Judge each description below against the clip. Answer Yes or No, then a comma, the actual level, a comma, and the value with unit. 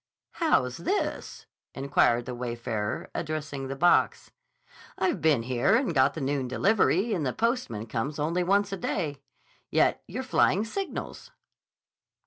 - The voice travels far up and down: Yes, wide, 7.8 semitones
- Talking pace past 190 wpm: No, slow, 135 wpm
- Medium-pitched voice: Yes, medium, 150 Hz